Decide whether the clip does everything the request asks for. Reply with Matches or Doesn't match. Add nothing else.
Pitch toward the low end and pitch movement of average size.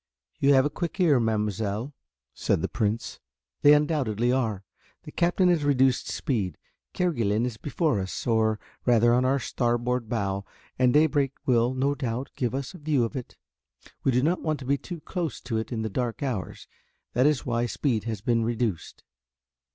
Matches